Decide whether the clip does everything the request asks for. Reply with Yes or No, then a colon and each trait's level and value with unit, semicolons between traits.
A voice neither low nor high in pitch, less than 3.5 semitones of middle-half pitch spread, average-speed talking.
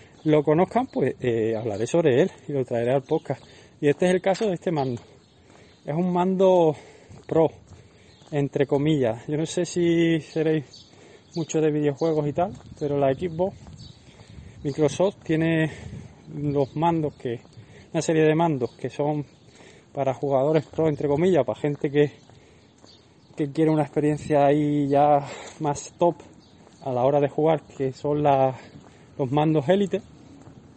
Yes: medium, 145 Hz; average, 3.1 semitones; average, 150 wpm